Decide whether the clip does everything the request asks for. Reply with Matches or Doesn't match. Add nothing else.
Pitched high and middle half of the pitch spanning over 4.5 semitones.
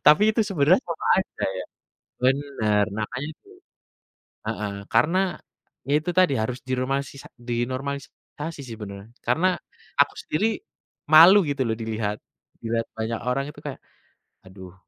Doesn't match